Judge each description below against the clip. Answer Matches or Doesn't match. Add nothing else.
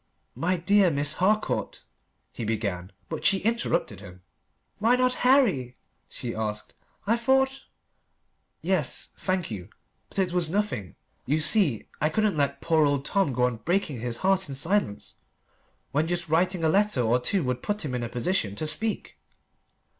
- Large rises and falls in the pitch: Matches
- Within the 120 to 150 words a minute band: Doesn't match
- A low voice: Doesn't match